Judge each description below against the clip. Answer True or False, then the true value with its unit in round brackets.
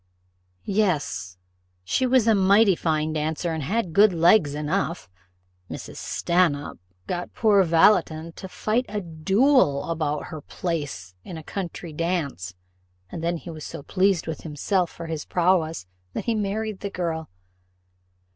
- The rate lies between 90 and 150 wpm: True (145 wpm)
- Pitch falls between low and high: True (170 Hz)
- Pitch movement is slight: False (4.1 semitones)